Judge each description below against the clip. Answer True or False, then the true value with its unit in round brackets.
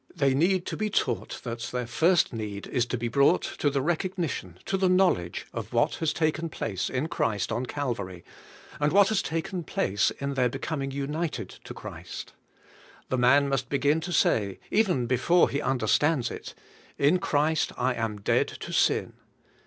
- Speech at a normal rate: True (175 wpm)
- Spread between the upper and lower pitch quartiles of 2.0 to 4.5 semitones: False (5.3 semitones)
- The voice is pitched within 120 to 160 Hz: True (140 Hz)